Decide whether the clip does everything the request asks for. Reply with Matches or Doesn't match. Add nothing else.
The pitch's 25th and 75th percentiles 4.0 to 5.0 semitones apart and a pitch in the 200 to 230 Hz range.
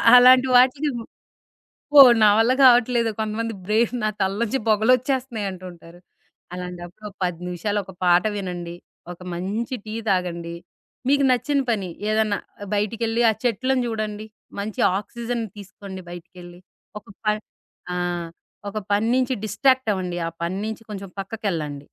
Matches